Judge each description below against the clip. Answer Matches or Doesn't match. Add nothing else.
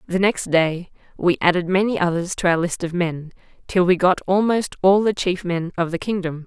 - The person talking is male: Doesn't match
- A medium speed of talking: Doesn't match